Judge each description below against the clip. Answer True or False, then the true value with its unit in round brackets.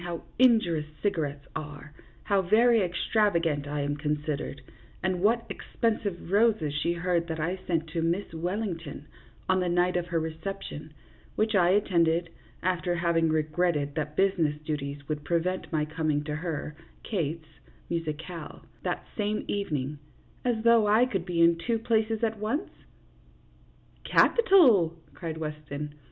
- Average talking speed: True (150 wpm)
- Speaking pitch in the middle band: True (170 Hz)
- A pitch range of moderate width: True (4.6 semitones)